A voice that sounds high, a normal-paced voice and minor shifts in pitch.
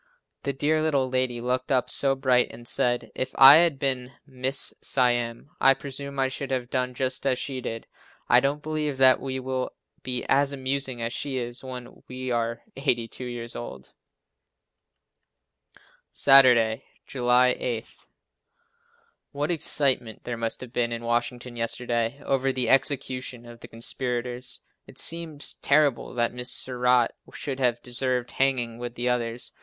No: low, 125 Hz; average, 150 wpm; narrow, 2.0 semitones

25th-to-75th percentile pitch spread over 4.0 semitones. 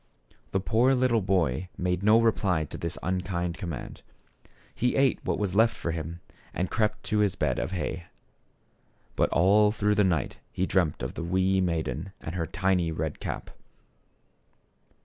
No: average, 3.7 semitones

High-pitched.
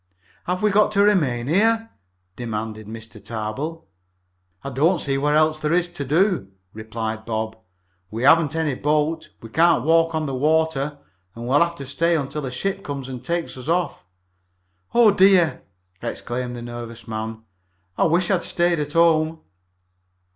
No: medium, 150 Hz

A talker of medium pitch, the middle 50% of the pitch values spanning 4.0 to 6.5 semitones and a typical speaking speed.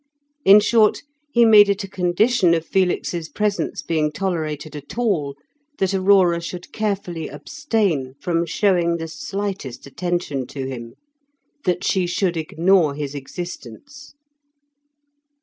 No: medium, 175 Hz; average, 4.4 semitones; slow, 125 wpm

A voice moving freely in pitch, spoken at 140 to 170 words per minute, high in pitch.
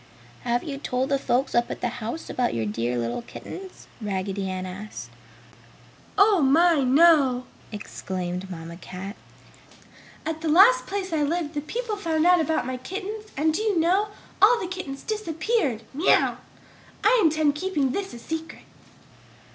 Yes: wide, 7.5 semitones; average, 155 wpm; very high, 295 Hz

